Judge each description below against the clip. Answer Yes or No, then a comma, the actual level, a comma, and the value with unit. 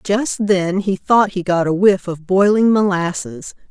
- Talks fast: No, average, 180 wpm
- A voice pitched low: No, high, 190 Hz